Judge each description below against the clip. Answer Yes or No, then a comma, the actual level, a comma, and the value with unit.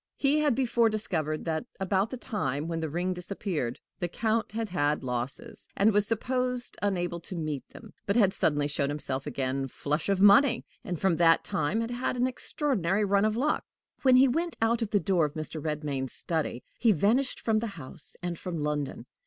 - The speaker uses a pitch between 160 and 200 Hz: Yes, high, 190 Hz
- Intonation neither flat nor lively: No, wide, 7.0 semitones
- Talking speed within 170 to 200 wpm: Yes, average, 195 wpm